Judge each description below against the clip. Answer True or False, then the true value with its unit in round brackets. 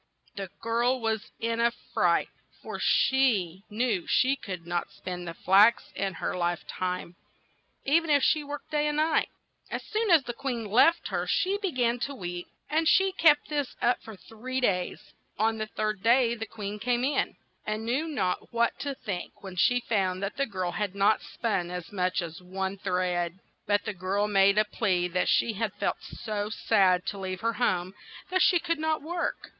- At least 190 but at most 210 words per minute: True (195 wpm)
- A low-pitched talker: False (215 Hz)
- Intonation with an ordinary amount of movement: False (5.9 semitones)